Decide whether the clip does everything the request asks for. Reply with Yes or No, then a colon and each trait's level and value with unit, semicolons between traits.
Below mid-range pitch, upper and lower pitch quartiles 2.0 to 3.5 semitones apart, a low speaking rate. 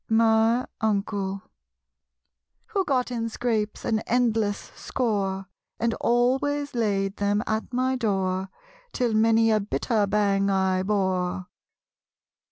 No: high, 220 Hz; average, 3.2 semitones; slow, 110 wpm